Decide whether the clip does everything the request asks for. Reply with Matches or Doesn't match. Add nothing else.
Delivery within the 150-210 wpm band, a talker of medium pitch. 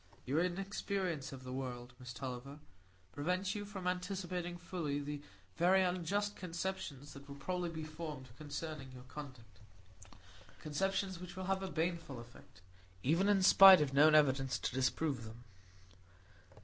Doesn't match